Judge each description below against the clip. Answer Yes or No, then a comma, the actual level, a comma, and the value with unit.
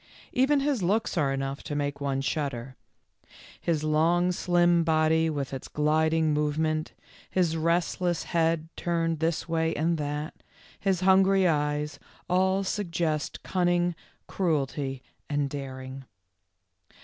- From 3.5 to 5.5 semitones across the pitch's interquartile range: No, average, 3.0 semitones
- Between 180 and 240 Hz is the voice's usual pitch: No, medium, 160 Hz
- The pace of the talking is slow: Yes, slow, 120 wpm